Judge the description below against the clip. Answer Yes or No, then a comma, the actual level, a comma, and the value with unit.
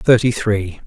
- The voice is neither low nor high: No, low, 110 Hz